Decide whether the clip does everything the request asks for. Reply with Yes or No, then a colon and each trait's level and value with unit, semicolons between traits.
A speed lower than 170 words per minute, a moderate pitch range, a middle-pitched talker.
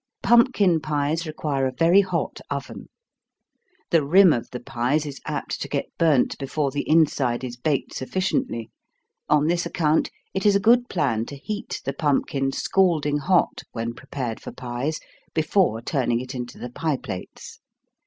Yes: average, 160 wpm; average, 4.7 semitones; medium, 145 Hz